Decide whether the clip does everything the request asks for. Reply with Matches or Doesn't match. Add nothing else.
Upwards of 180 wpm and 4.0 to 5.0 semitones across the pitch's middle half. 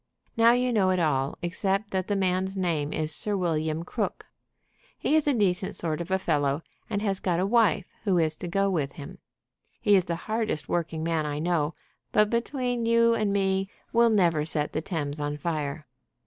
Matches